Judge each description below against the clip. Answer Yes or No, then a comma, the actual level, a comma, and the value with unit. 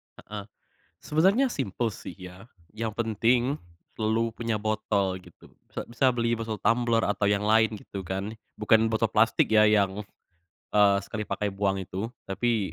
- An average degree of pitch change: No, narrow, 2.3 semitones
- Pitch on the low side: Yes, low, 110 Hz